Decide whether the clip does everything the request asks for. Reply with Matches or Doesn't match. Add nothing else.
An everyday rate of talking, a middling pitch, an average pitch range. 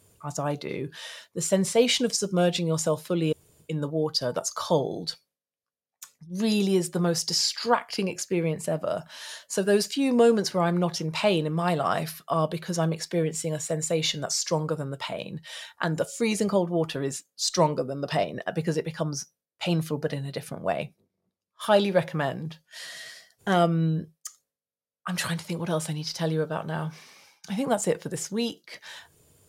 Matches